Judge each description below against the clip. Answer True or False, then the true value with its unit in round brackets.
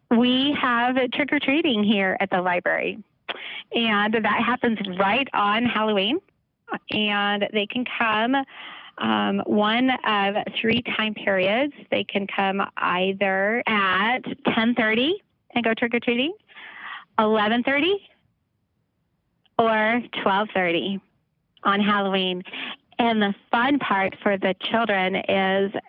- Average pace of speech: False (105 wpm)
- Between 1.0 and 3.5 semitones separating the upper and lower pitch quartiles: False (3.9 semitones)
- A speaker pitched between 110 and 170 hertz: False (215 Hz)